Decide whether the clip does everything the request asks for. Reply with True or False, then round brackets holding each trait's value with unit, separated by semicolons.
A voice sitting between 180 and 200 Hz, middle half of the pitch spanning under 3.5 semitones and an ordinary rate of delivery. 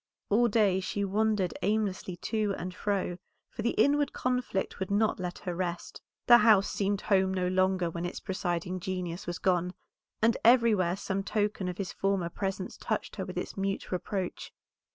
True (190 Hz; 2.5 semitones; 175 wpm)